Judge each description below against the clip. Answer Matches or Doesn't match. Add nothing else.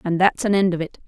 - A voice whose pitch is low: Doesn't match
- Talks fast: Matches